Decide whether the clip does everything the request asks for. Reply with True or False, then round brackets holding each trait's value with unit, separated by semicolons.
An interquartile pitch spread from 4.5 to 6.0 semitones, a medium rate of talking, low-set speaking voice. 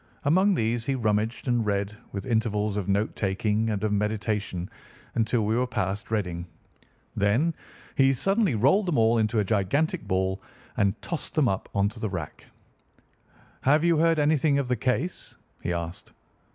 True (5.0 semitones; 165 wpm; 110 Hz)